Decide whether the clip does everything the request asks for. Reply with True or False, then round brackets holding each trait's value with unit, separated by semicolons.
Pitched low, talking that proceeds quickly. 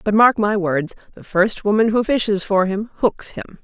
False (205 Hz; 215 wpm)